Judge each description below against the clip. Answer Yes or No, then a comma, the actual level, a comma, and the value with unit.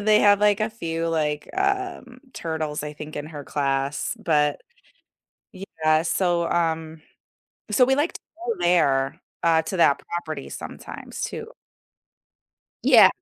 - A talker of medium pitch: Yes, medium, 165 Hz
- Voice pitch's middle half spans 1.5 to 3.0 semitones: No, wide, 5.4 semitones